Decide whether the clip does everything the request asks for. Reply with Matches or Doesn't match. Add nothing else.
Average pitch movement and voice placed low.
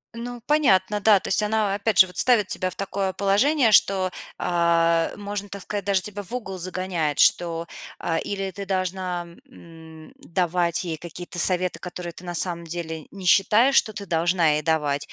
Doesn't match